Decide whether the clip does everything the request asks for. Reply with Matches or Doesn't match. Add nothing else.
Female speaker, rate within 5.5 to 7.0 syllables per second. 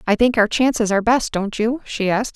Matches